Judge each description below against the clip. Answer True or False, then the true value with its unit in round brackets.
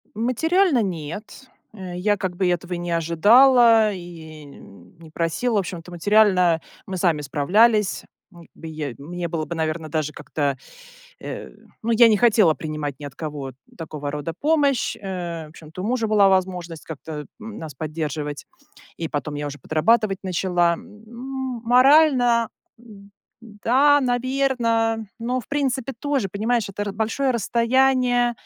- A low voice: False (190 Hz)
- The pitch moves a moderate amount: False (6.6 semitones)